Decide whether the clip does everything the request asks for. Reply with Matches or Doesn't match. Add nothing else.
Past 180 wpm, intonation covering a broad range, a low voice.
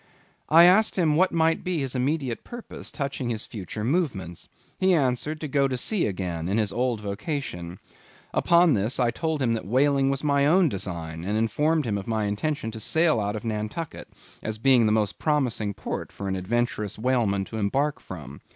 Matches